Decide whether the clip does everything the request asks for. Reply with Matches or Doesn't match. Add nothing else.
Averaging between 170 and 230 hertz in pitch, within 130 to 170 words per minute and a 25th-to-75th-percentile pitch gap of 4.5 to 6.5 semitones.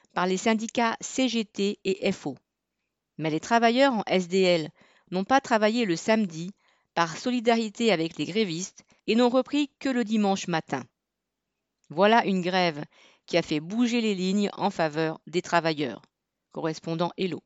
Matches